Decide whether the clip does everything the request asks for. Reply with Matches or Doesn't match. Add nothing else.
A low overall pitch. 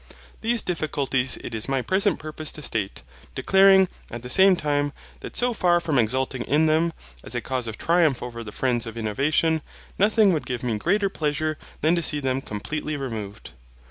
Doesn't match